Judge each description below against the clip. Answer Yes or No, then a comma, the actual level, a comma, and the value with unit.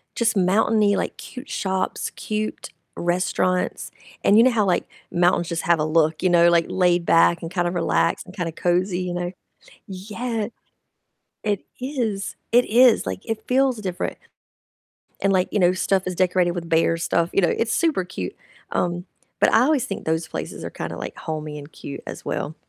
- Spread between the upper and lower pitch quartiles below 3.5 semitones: No, average, 3.8 semitones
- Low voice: No, medium, 185 Hz